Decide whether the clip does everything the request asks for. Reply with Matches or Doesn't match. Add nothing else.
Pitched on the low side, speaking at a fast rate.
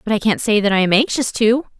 Doesn't match